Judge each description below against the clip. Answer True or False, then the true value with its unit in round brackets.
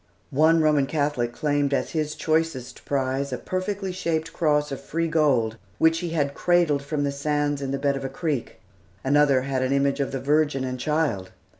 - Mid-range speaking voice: True (145 Hz)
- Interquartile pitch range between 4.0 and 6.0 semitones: False (2.5 semitones)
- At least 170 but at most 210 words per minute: True (190 wpm)